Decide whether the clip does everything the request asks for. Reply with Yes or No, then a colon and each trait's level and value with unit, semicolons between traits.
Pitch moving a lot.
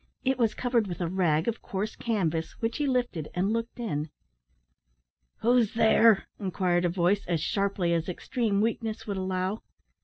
No: average, 4.4 semitones